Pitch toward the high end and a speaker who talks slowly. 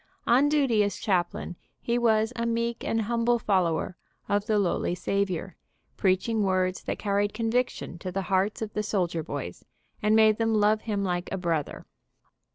No: high, 205 Hz; average, 175 wpm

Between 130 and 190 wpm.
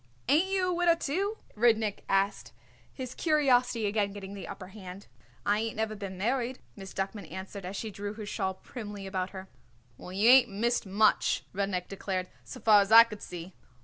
Yes: average, 185 wpm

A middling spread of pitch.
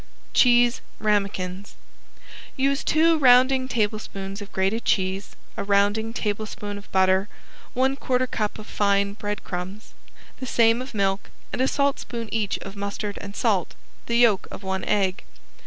Yes: average, 3.4 semitones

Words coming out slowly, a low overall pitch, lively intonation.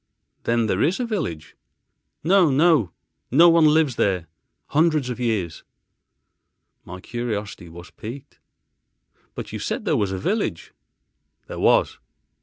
Yes: slow, 130 wpm; low, 120 Hz; wide, 8.8 semitones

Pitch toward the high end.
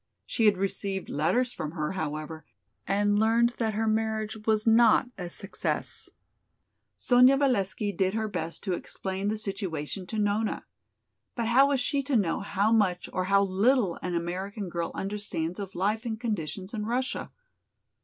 Yes: high, 205 Hz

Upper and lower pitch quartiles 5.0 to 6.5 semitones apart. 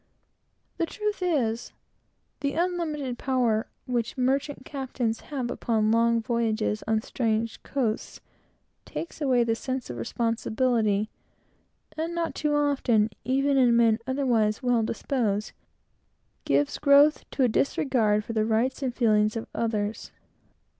No: average, 3.8 semitones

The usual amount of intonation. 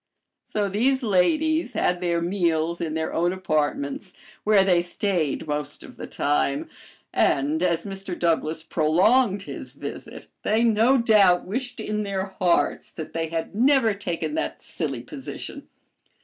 Yes: average, 4.6 semitones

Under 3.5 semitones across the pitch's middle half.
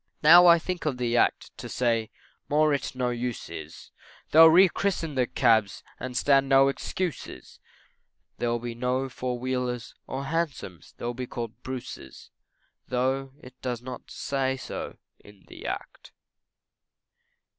Yes: narrow, 2.5 semitones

